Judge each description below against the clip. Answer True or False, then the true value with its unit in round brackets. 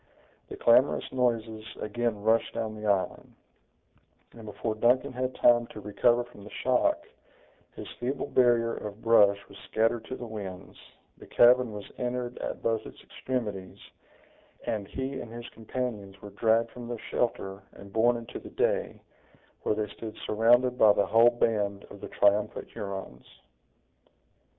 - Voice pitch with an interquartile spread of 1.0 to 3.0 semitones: True (2.7 semitones)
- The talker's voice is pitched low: True (115 Hz)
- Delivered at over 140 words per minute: True (155 wpm)